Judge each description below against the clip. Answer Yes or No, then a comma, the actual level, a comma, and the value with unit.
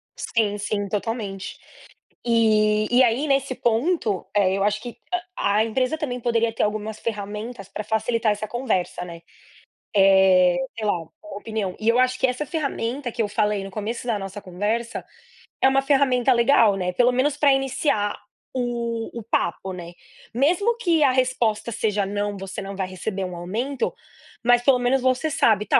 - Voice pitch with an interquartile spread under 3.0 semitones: No, average, 3.9 semitones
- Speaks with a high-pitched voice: Yes, high, 225 Hz